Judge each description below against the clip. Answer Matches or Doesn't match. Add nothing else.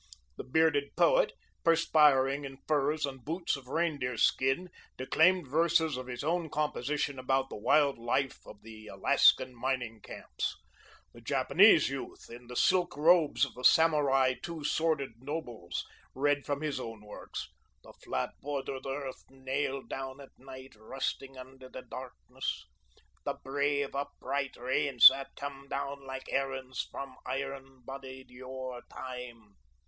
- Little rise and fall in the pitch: Matches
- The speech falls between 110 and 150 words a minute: Matches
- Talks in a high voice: Doesn't match